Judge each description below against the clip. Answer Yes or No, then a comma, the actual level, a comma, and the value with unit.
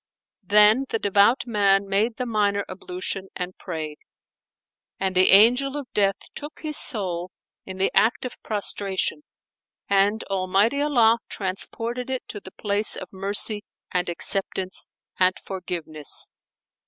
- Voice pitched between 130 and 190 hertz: No, high, 200 Hz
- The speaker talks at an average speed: No, slow, 130 wpm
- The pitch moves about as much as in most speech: Yes, average, 3.2 semitones